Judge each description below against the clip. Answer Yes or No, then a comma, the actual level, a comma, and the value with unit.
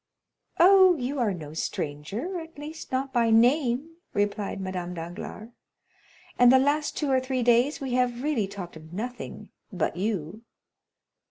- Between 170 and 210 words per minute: No, average, 145 wpm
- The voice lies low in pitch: No, high, 240 Hz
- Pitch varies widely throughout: Yes, wide, 6.3 semitones